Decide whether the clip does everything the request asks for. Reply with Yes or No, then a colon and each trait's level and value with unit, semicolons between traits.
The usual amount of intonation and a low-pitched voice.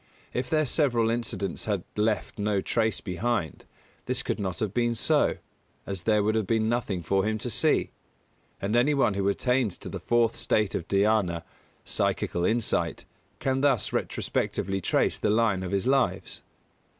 Yes: average, 3.3 semitones; low, 110 Hz